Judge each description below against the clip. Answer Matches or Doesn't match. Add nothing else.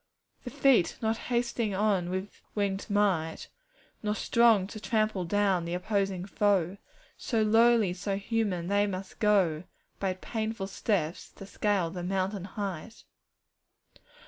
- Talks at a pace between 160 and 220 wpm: Doesn't match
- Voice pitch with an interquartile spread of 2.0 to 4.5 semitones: Matches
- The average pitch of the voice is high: Matches